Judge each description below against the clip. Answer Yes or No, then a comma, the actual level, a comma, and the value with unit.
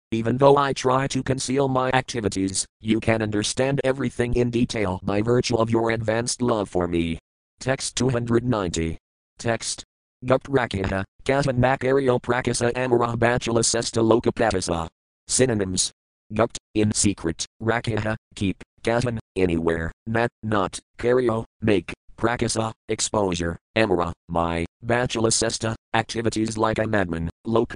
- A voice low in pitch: Yes, low, 115 Hz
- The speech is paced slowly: Yes, slow, 130 wpm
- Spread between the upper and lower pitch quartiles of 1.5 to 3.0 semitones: No, average, 4.1 semitones